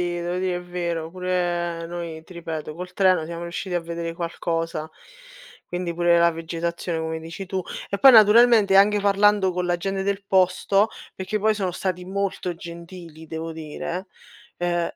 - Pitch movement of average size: No, narrow, 2.2 semitones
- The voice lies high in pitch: No, medium, 175 Hz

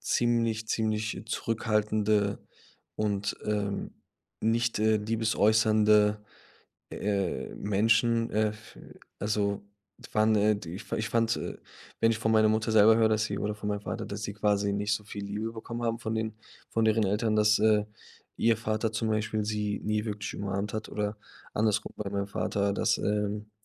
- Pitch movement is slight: Yes, narrow, 1.2 semitones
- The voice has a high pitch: No, low, 105 Hz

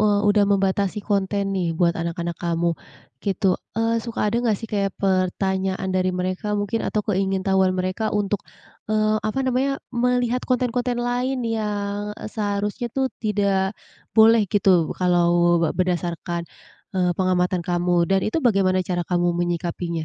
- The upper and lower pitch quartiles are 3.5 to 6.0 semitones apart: No, average, 3.1 semitones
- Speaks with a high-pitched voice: Yes, high, 195 Hz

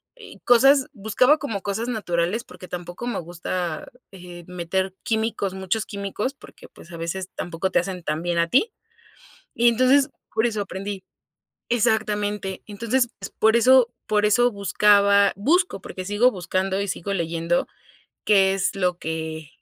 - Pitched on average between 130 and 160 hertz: No, high, 200 Hz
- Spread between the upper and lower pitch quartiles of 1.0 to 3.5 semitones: No, average, 4.2 semitones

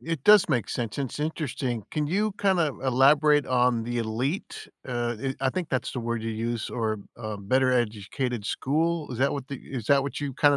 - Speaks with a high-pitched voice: No, low, 130 Hz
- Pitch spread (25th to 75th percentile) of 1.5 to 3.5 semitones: No, average, 4.0 semitones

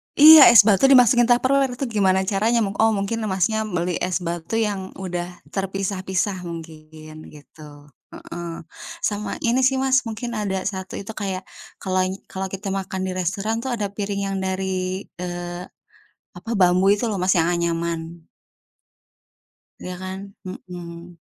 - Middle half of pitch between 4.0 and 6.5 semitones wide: No, average, 3.2 semitones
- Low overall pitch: No, high, 190 Hz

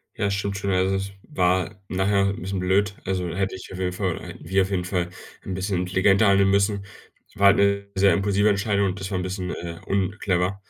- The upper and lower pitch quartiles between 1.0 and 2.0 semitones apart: Yes, narrow, 1.4 semitones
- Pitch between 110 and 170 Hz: No, very low, 95 Hz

